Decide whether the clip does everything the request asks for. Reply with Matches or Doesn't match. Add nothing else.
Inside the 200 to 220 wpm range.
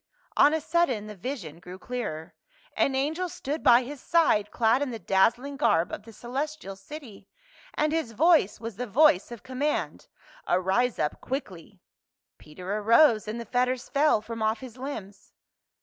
Doesn't match